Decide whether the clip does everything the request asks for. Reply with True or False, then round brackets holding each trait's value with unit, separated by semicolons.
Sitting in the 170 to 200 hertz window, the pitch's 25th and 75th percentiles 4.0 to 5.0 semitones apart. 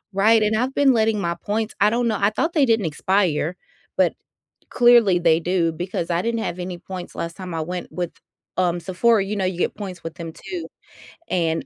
True (190 Hz; 4.3 semitones)